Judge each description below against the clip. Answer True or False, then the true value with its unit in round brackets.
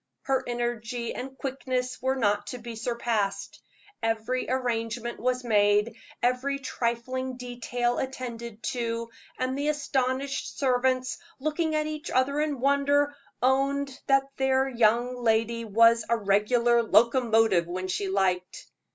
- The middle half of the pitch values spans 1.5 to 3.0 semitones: True (2.6 semitones)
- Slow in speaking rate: True (125 wpm)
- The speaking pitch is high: True (245 Hz)